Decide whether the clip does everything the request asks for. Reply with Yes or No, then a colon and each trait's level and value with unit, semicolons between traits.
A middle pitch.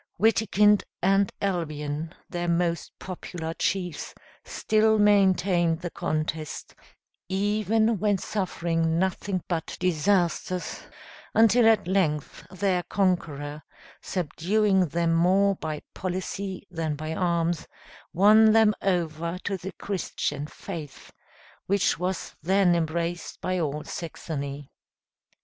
Yes: medium, 180 Hz